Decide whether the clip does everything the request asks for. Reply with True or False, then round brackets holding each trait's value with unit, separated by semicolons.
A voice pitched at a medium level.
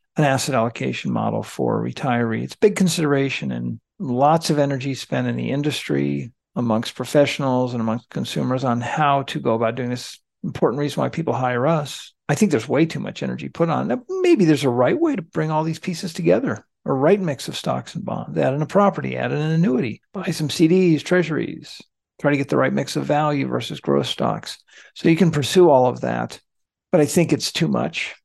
True (145 Hz)